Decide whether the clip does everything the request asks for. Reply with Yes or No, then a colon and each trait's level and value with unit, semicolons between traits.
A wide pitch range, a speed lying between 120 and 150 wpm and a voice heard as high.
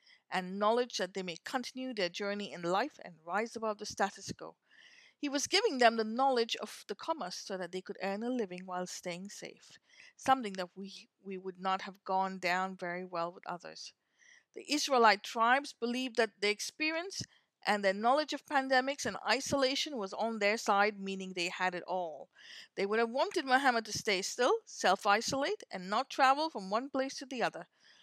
No: wide, 5.7 semitones; average, 195 wpm; high, 215 Hz